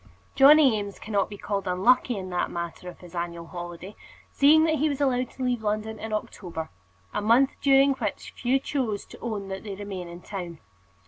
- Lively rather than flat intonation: Yes, wide, 5.9 semitones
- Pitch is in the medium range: No, high, 210 Hz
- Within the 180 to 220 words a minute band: Yes, average, 195 wpm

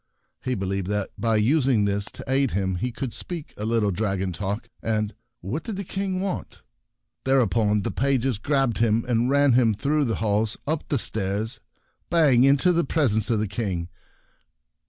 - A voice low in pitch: Yes, low, 115 Hz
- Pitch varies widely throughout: No, average, 4.9 semitones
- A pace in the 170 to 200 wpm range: Yes, average, 175 wpm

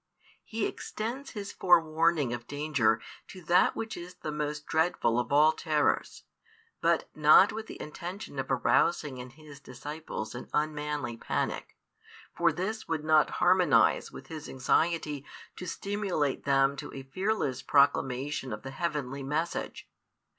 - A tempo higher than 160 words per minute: No, average, 145 wpm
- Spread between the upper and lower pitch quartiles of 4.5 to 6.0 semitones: No, average, 4.1 semitones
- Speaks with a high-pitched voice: No, medium, 150 Hz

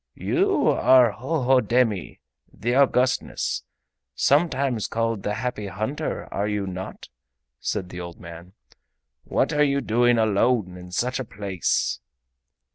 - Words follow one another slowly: Yes, slow, 120 wpm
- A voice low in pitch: Yes, low, 115 Hz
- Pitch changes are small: No, average, 4.6 semitones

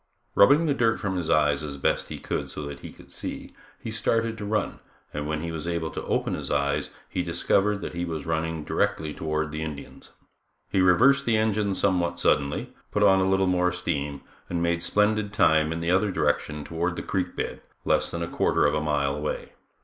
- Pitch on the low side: Yes, very low, 85 Hz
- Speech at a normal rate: No, fast, 210 wpm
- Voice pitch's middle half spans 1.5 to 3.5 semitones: No, average, 4.2 semitones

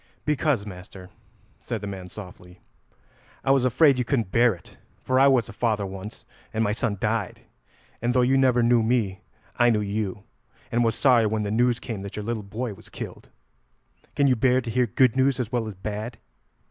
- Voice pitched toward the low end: Yes, low, 115 Hz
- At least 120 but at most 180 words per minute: No, average, 200 wpm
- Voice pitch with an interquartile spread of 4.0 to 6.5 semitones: No, average, 3.4 semitones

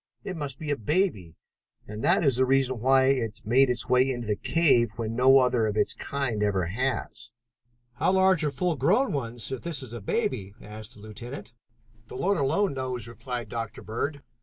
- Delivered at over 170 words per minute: Yes, average, 195 wpm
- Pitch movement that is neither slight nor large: Yes, average, 3.7 semitones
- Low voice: Yes, low, 125 Hz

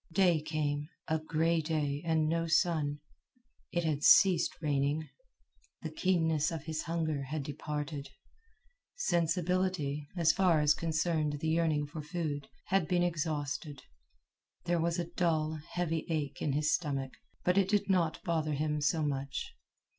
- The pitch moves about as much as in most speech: No, narrow, 2.3 semitones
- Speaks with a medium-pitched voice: Yes, medium, 155 Hz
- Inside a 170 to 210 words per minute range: No, average, 145 wpm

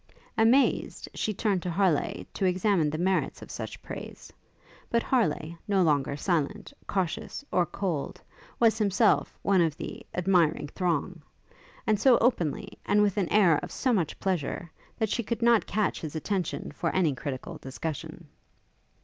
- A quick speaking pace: No, average, 155 wpm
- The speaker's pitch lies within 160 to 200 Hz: Yes, medium, 185 Hz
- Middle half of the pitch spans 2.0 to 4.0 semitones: No, average, 4.6 semitones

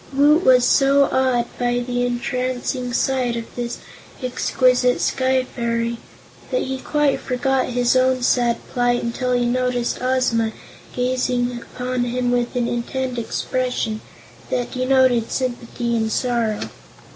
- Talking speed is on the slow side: Yes, slow, 130 wpm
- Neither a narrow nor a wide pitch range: No, narrow, 1.2 semitones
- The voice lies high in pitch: Yes, very high, 250 Hz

